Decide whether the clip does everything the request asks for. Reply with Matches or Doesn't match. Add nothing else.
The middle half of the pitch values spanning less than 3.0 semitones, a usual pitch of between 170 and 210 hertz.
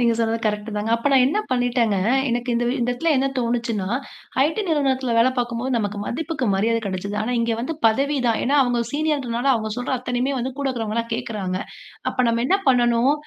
Doesn't match